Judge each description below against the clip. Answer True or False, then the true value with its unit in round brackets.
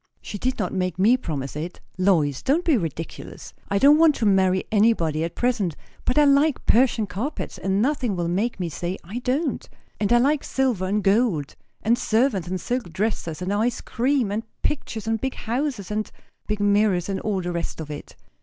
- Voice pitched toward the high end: True (210 Hz)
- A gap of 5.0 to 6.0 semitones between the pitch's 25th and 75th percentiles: True (5.5 semitones)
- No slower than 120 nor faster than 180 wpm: False (195 wpm)